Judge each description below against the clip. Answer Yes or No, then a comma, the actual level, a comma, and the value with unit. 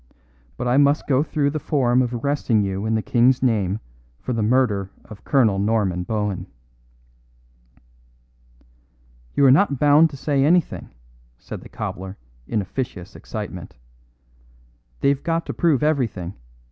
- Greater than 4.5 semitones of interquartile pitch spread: Yes, wide, 5.5 semitones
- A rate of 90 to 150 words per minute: Yes, average, 140 wpm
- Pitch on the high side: No, low, 120 Hz